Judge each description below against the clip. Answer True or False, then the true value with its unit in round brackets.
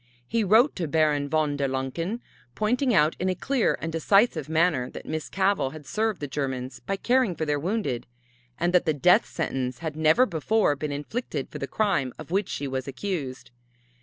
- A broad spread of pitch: True (5.9 semitones)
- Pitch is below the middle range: False (160 Hz)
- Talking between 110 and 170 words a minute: False (190 wpm)